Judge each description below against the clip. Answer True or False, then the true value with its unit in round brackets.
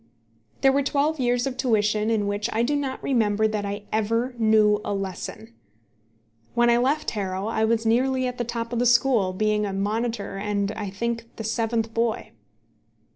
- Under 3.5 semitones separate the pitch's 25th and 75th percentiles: True (2.7 semitones)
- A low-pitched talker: False (225 Hz)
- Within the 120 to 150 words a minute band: False (180 wpm)